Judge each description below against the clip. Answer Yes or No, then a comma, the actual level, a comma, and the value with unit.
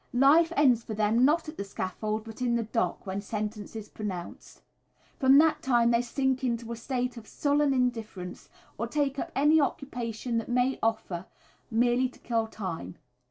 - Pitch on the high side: Yes, high, 235 Hz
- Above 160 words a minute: Yes, average, 175 wpm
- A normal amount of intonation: Yes, average, 3.5 semitones